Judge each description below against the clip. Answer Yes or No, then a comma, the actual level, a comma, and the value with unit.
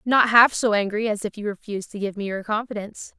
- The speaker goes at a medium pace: No, fast, 245 wpm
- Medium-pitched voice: No, high, 210 Hz